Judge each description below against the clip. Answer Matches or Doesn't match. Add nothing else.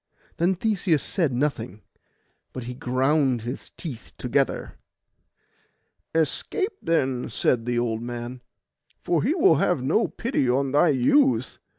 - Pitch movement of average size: Doesn't match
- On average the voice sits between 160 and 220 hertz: Doesn't match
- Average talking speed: Doesn't match